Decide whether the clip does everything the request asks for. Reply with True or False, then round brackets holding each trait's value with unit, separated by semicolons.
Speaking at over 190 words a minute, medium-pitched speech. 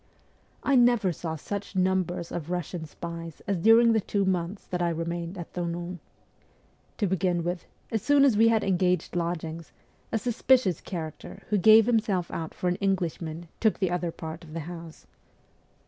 False (170 wpm; 180 Hz)